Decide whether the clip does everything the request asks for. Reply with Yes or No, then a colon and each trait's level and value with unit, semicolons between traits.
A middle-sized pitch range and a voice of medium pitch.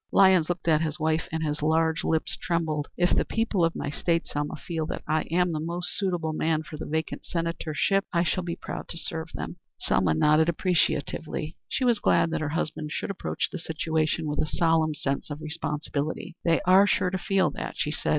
No: narrow, 2.1 semitones; medium, 160 Hz